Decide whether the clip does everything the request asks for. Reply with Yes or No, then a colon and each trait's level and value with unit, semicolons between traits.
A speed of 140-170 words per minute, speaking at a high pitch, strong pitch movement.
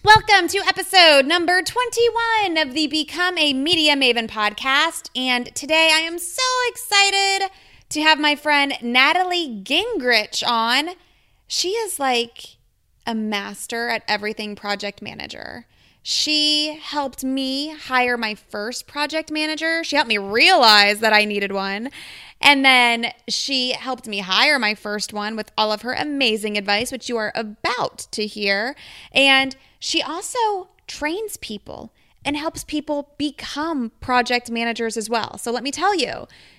Yes: average, 145 wpm; very high, 275 Hz; wide, 6.1 semitones